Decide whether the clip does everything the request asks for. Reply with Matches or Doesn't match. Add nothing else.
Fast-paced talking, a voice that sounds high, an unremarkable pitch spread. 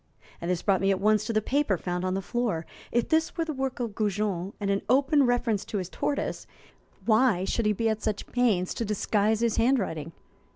Matches